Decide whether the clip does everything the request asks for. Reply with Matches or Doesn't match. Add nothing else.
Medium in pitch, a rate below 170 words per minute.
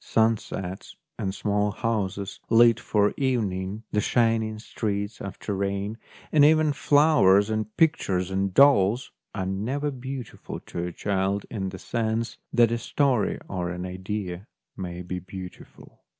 Doesn't match